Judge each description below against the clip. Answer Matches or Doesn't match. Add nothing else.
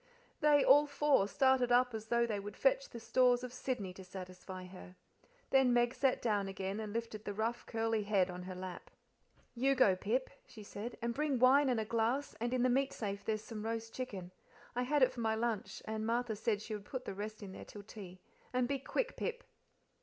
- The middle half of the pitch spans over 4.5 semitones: Doesn't match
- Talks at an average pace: Doesn't match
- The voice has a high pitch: Matches